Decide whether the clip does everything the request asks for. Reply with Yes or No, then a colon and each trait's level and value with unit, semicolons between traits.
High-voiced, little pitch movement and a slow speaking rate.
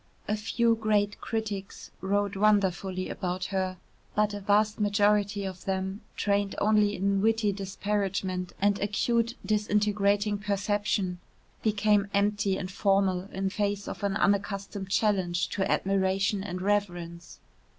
Yes: high, 200 Hz; narrow, 1.4 semitones; slow, 125 wpm